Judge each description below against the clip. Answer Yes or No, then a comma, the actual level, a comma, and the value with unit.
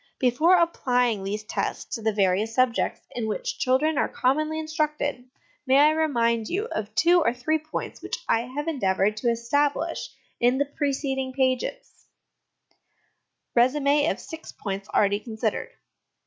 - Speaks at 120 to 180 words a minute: Yes, average, 145 wpm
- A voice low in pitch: No, very high, 255 Hz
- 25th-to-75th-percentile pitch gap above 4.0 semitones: Yes, average, 5.1 semitones